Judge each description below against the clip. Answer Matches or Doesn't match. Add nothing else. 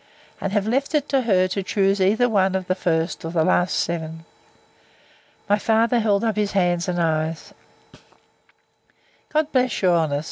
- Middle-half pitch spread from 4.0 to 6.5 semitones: Matches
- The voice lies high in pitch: Matches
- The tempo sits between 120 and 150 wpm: Doesn't match